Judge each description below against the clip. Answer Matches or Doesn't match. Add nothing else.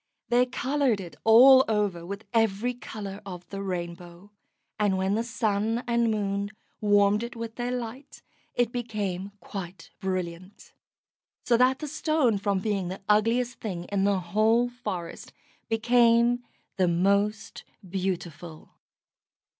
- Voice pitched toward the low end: Doesn't match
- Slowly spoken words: Matches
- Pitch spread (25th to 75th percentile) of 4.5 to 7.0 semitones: Doesn't match